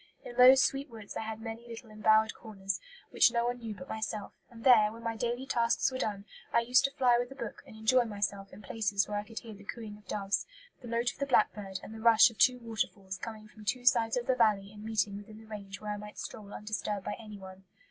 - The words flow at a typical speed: No, fast, 250 wpm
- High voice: Yes, high, 220 Hz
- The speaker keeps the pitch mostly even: Yes, narrow, 2.3 semitones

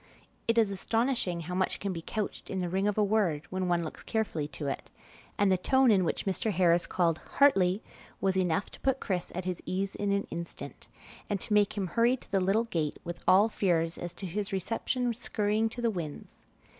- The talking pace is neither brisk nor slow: No, fast, 215 wpm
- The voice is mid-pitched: No, high, 195 Hz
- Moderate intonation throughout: Yes, average, 3.6 semitones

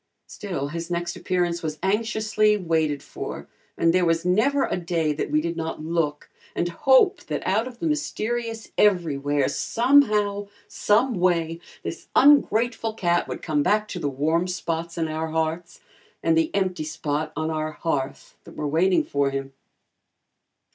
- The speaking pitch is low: No, medium, 170 Hz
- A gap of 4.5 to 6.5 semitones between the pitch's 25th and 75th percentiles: Yes, average, 5.0 semitones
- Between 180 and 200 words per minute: No, average, 155 wpm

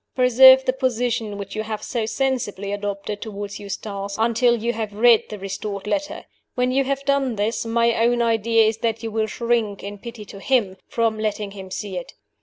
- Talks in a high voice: Yes, high, 225 Hz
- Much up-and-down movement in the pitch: No, average, 2.8 semitones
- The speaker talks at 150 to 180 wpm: No, average, 195 wpm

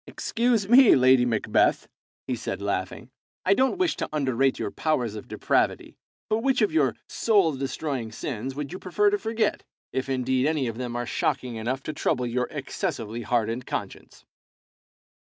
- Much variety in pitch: Yes, wide, 7.5 semitones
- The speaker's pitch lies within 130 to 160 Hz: Yes, low, 135 Hz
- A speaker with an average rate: Yes, average, 165 wpm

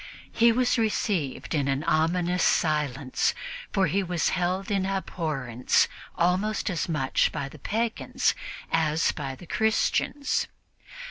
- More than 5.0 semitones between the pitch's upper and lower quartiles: No, average, 4.7 semitones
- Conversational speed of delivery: No, slow, 125 wpm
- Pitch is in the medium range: Yes, medium, 175 Hz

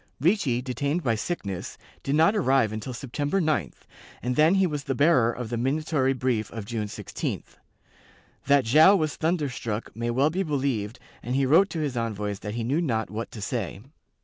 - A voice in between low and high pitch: No, low, 130 Hz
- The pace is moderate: Yes, average, 185 wpm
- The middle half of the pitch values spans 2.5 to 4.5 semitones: No, average, 5.1 semitones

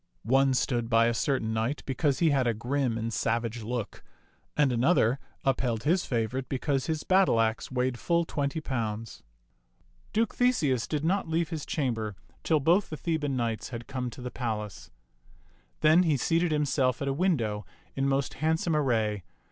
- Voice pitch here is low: Yes, low, 130 Hz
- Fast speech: No, average, 175 wpm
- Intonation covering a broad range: No, average, 4.9 semitones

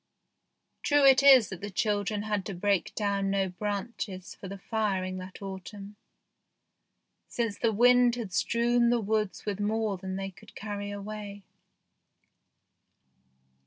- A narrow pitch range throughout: Yes, narrow, 2.3 semitones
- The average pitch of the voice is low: No, high, 205 Hz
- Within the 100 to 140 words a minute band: Yes, slow, 135 wpm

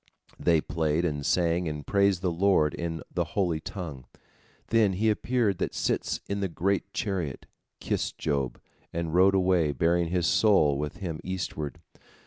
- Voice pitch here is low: Yes, very low, 85 Hz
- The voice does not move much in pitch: No, average, 3.8 semitones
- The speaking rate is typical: Yes, average, 155 wpm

